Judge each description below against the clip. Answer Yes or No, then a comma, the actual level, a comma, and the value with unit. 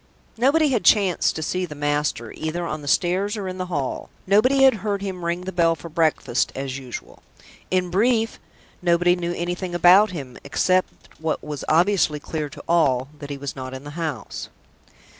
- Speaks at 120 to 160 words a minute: No, average, 185 wpm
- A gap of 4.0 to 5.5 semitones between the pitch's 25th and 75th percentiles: Yes, average, 4.3 semitones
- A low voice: No, medium, 170 Hz